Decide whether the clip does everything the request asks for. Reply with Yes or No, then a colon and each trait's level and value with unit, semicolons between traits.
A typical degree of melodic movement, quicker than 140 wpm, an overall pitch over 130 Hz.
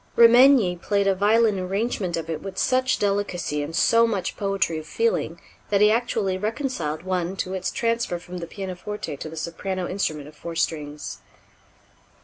Yes: average, 4.2 semitones; average, 165 wpm; high, 190 Hz